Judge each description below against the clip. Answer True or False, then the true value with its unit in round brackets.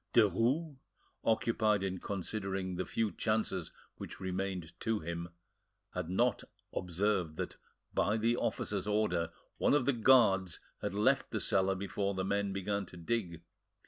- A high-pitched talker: False (100 Hz)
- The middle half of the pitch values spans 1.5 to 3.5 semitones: True (3.1 semitones)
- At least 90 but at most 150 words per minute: True (145 wpm)